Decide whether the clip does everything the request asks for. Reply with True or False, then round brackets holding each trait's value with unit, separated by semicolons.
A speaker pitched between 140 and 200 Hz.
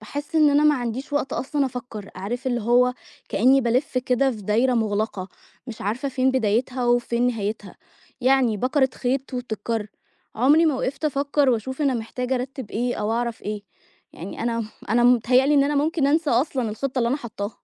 False (250 Hz)